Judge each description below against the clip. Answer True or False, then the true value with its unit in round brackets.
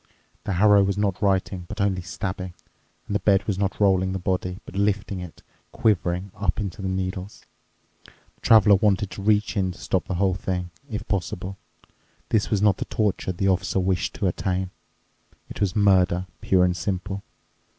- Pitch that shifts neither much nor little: False (1.7 semitones)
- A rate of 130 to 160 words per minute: False (180 wpm)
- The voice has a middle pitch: False (95 Hz)